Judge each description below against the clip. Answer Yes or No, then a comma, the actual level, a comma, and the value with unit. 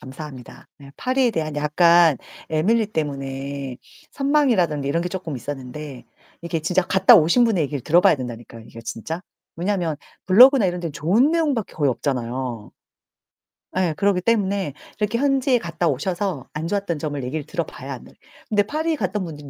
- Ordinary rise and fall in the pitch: No, wide, 6.2 semitones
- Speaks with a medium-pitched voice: Yes, medium, 170 Hz